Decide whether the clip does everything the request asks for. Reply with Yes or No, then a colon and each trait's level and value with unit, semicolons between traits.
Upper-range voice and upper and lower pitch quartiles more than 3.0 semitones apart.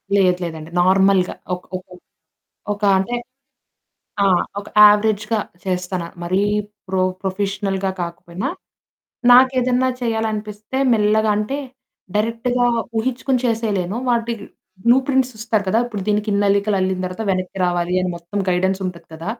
Yes: high, 205 Hz; average, 3.4 semitones